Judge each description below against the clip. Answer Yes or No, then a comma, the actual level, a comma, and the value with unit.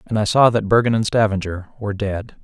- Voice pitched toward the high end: No, low, 105 Hz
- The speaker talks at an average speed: No, fast, 220 wpm